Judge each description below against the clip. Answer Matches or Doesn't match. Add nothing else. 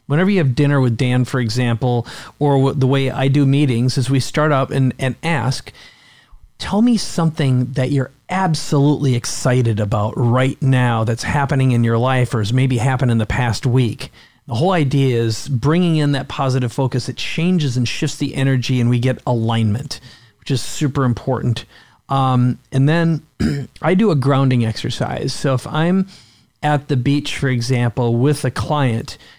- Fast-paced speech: Doesn't match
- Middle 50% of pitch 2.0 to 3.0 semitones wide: Matches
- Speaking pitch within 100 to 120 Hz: Doesn't match